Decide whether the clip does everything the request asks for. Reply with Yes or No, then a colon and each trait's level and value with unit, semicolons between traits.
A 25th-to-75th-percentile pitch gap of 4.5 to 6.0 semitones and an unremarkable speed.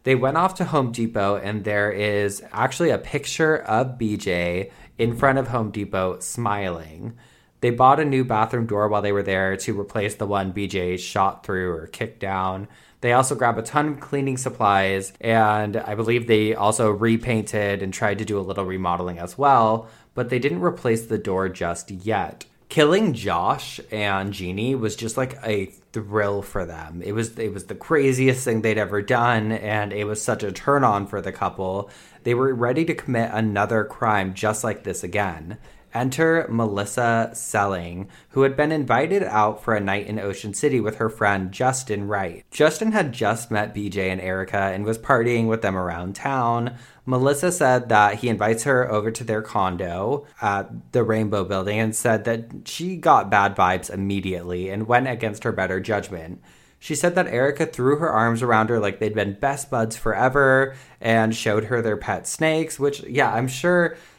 No: average, 3.8 semitones; average, 185 wpm